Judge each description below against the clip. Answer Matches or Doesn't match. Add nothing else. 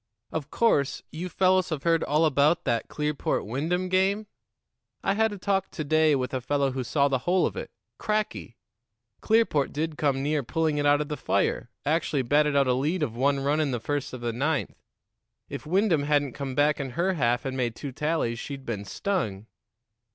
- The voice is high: Doesn't match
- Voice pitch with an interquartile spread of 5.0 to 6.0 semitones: Doesn't match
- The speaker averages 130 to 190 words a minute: Doesn't match